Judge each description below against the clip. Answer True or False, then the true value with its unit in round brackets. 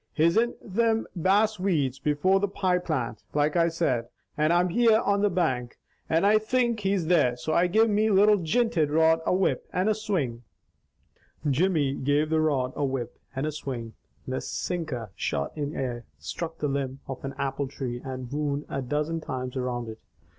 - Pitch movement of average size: False (6.1 semitones)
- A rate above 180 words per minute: True (190 wpm)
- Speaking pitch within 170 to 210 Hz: False (155 Hz)